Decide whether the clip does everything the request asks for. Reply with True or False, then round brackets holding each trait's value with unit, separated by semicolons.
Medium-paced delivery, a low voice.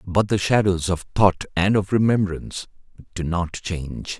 True (155 wpm; 95 Hz)